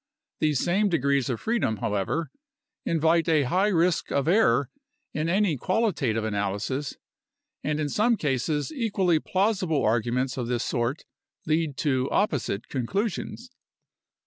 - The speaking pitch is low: No, medium, 155 Hz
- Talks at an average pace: No, slow, 125 wpm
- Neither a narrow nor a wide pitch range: No, wide, 6.4 semitones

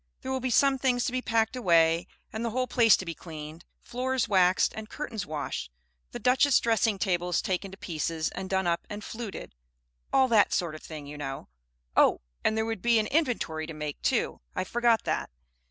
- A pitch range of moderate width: No, wide, 6.2 semitones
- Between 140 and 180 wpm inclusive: No, fast, 205 wpm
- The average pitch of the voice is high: Yes, high, 205 Hz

